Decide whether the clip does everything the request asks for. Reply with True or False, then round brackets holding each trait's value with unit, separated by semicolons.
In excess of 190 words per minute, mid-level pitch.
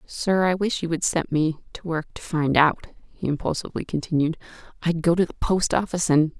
True (205 wpm; 165 Hz)